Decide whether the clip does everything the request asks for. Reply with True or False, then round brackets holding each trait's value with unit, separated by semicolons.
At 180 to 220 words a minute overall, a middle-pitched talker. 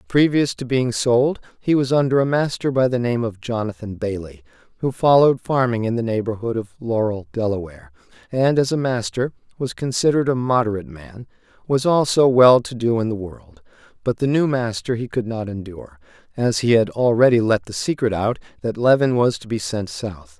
False (185 wpm; 115 Hz)